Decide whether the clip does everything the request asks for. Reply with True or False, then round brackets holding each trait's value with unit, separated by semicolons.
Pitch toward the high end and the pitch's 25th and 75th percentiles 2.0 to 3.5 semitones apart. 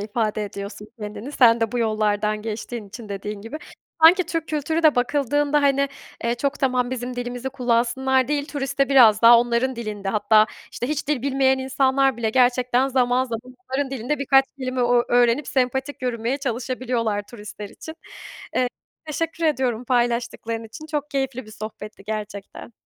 True (245 Hz; 3.2 semitones)